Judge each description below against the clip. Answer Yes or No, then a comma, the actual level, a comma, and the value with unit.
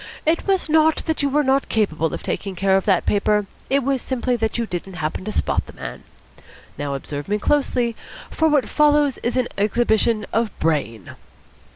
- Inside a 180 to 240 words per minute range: Yes, average, 190 wpm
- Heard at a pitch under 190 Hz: No, high, 225 Hz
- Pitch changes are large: Yes, wide, 6.3 semitones